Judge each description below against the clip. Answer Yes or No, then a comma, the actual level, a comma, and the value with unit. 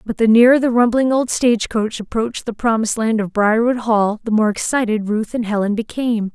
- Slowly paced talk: No, average, 200 wpm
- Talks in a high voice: Yes, high, 225 Hz